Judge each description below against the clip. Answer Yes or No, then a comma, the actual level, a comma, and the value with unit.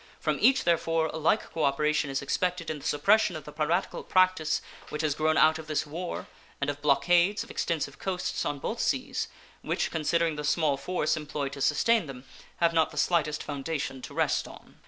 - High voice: No, medium, 155 Hz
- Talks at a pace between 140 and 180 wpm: No, average, 195 wpm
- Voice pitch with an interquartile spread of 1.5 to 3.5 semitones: Yes, average, 2.7 semitones